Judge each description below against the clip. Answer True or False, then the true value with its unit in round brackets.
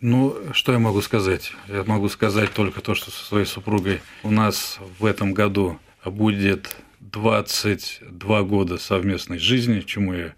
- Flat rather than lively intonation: True (1.9 semitones)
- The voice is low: True (100 Hz)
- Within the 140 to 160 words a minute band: True (150 wpm)